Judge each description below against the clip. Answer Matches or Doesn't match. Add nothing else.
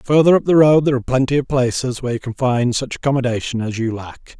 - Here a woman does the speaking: Doesn't match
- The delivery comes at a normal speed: Doesn't match